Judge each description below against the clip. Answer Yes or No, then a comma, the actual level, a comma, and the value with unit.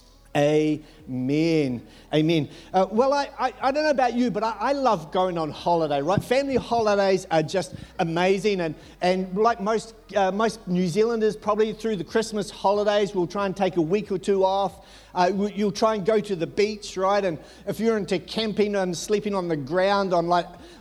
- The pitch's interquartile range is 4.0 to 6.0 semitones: No, average, 3.5 semitones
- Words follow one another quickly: No, average, 195 wpm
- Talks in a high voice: Yes, high, 195 Hz